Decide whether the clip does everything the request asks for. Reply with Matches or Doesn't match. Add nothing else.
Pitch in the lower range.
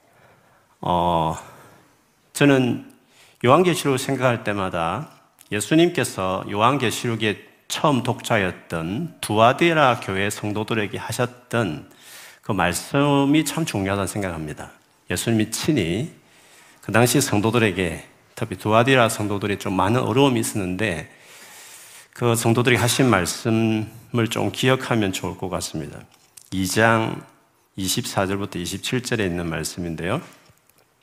Matches